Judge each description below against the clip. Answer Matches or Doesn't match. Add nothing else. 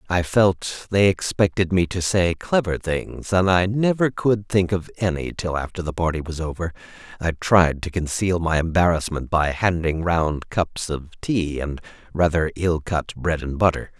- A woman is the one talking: Doesn't match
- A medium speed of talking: Matches